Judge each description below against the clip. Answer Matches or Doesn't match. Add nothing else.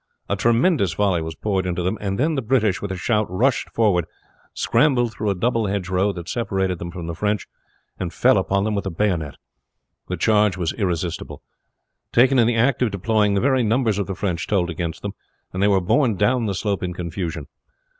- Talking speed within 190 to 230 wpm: Matches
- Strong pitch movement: Doesn't match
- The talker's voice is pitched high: Doesn't match